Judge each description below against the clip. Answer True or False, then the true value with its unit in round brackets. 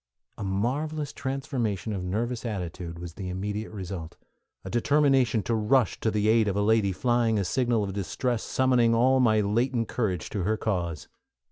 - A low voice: True (110 Hz)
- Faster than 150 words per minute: True (170 wpm)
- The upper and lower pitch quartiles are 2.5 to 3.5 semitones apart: False (3.9 semitones)